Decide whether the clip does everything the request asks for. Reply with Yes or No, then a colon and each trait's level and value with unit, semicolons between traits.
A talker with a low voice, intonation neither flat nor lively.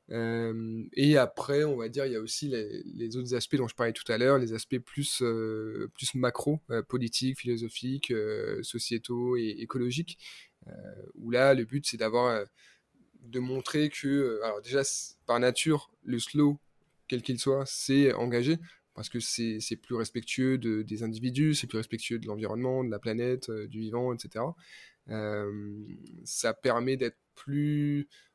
Yes: low, 125 Hz; average, 3.4 semitones